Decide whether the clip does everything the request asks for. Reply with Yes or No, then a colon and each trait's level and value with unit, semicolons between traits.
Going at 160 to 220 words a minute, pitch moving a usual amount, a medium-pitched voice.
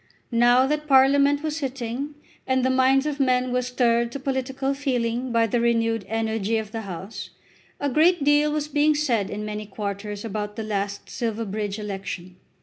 No: average, 170 wpm; average, 4.2 semitones; high, 240 Hz